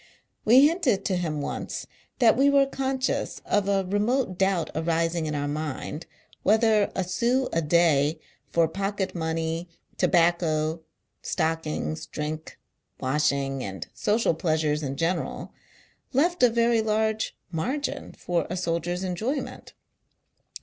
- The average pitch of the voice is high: No, medium, 175 Hz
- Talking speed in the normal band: No, slow, 125 wpm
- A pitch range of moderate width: No, wide, 5.7 semitones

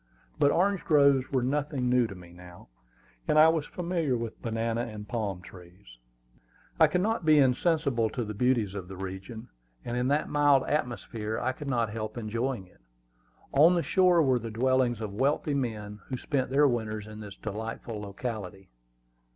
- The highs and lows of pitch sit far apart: No, average, 4.9 semitones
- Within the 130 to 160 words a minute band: No, average, 175 wpm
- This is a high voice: No, low, 120 Hz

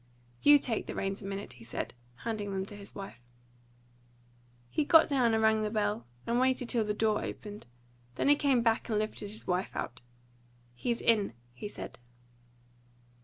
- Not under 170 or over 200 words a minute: Yes, average, 175 wpm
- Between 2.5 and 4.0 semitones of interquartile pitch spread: Yes, average, 2.9 semitones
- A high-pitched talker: Yes, high, 215 Hz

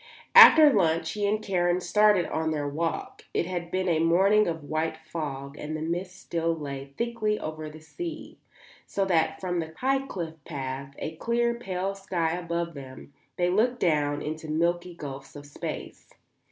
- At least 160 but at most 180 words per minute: Yes, average, 170 wpm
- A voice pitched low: No, medium, 170 Hz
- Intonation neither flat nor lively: Yes, average, 3.7 semitones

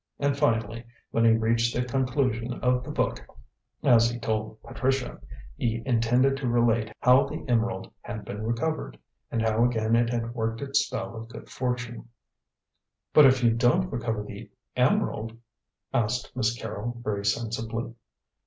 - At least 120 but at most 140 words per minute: No, average, 155 wpm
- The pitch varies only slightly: Yes, narrow, 1.8 semitones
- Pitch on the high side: No, low, 115 Hz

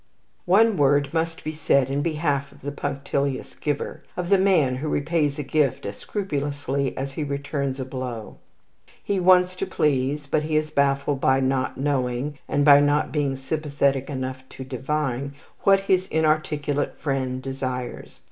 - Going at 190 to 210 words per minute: No, average, 160 wpm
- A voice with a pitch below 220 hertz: Yes, medium, 140 Hz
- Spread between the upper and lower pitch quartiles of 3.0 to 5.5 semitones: No, narrow, 2.4 semitones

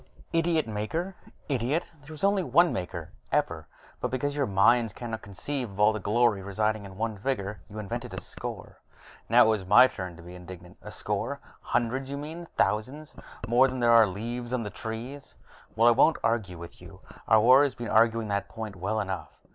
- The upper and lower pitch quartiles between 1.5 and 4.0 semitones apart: No, average, 4.5 semitones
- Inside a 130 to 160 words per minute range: No, average, 195 wpm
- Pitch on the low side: Yes, low, 115 Hz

